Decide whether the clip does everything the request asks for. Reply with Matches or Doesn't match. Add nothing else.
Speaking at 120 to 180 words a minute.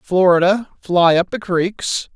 Matches